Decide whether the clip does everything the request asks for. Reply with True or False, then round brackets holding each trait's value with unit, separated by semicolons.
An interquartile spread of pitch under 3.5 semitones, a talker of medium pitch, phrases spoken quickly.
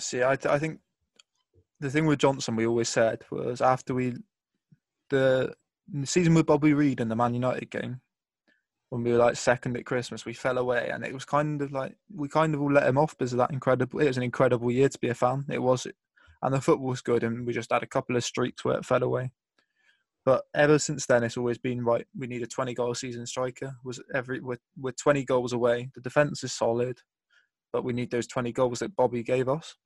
False (2.4 semitones; 125 Hz; 235 wpm)